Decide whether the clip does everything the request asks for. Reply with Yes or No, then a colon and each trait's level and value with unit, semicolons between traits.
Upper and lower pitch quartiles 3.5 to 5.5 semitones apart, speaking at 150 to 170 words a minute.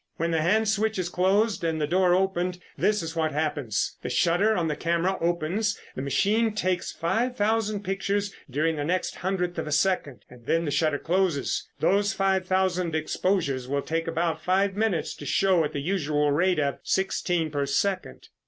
No: average, 3.8 semitones; average, 185 wpm